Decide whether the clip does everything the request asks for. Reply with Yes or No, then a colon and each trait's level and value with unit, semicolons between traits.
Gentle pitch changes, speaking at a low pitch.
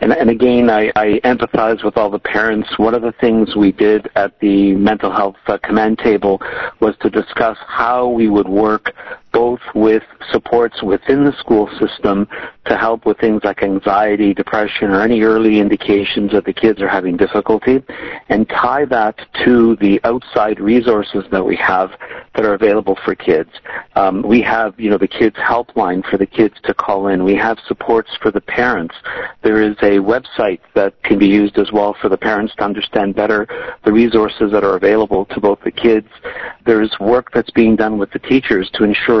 Yes: narrow, 2.1 semitones; low, 110 Hz